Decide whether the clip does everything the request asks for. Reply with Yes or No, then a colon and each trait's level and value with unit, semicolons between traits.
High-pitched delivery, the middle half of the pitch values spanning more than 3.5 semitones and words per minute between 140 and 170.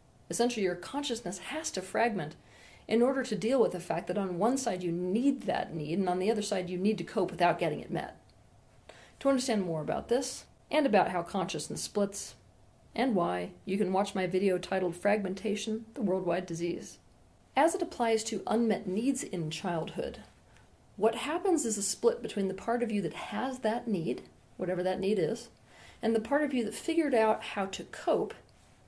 No: high, 205 Hz; average, 4.4 semitones; average, 195 wpm